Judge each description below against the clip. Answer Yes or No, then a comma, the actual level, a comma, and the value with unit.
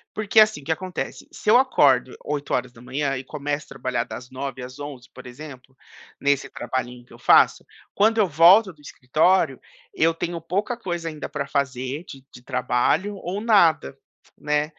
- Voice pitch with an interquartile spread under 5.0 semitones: No, wide, 5.5 semitones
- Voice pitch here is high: No, medium, 145 Hz